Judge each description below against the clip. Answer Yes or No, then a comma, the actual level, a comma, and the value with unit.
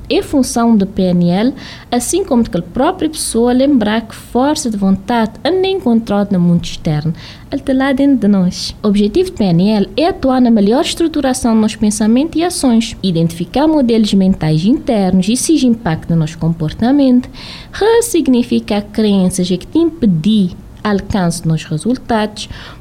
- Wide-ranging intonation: Yes, wide, 6.1 semitones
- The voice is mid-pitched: No, high, 225 Hz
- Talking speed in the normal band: Yes, average, 165 wpm